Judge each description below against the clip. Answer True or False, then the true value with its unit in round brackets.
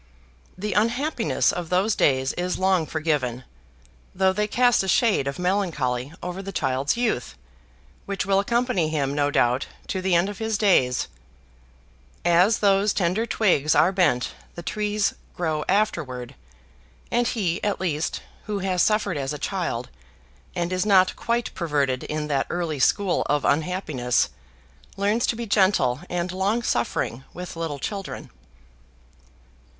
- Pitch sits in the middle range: True (180 Hz)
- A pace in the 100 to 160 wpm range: True (145 wpm)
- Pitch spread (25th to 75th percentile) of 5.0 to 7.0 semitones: True (5.5 semitones)